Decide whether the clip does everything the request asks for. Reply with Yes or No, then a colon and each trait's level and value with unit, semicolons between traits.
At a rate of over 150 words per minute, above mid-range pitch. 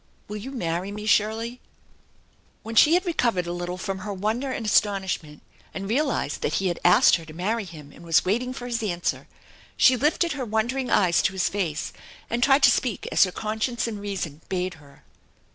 Yes: average, 200 wpm; high, 205 Hz